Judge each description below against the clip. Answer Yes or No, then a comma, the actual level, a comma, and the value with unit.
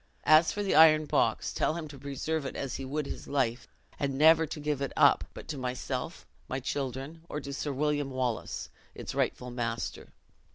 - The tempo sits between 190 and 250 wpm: Yes, average, 195 wpm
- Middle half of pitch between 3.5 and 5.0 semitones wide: No, average, 2.8 semitones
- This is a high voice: No, medium, 140 Hz